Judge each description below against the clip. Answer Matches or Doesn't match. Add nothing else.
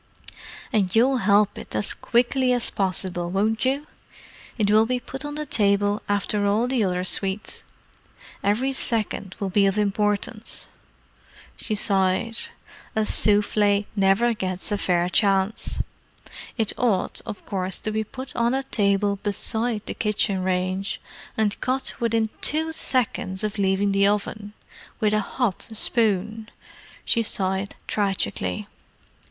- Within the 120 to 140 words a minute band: Matches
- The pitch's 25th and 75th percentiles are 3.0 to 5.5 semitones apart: Doesn't match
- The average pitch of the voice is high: Matches